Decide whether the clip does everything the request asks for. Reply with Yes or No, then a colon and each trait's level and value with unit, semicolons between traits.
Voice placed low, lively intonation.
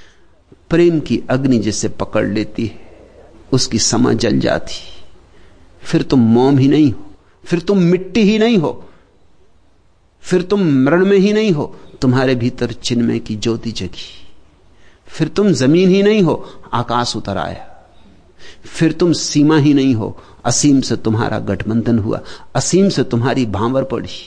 Yes: low, 125 Hz; wide, 7.0 semitones